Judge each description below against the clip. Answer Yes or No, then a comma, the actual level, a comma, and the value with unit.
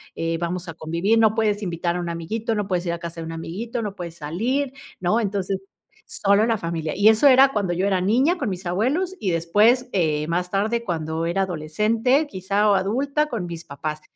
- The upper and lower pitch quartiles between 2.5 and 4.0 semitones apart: No, average, 4.8 semitones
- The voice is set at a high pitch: Yes, high, 195 Hz